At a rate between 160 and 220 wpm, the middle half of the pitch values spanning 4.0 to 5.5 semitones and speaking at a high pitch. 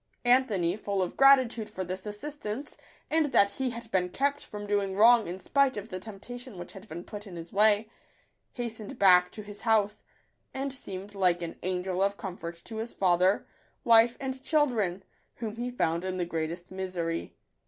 Yes: average, 185 wpm; average, 4.4 semitones; high, 205 Hz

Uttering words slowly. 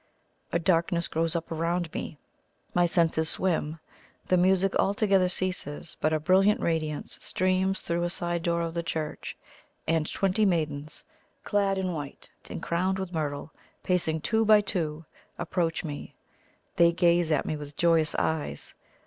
No: average, 150 wpm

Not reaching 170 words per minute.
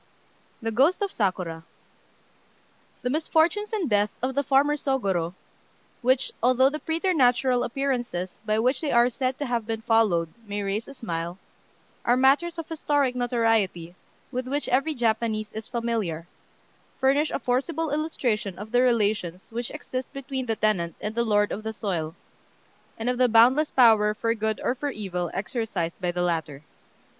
Yes: average, 160 wpm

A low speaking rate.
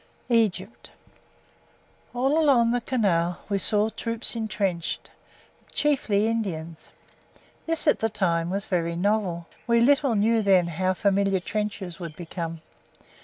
Yes: slow, 120 wpm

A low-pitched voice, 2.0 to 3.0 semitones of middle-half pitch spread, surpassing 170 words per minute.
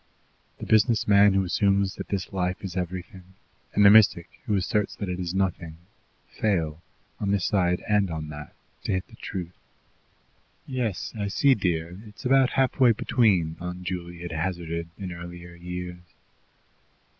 No: very low, 90 Hz; average, 2.7 semitones; average, 155 wpm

